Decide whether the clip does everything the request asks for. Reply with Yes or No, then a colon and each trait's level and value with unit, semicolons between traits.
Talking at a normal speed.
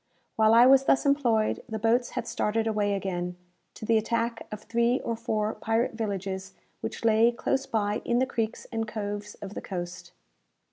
Yes: average, 180 wpm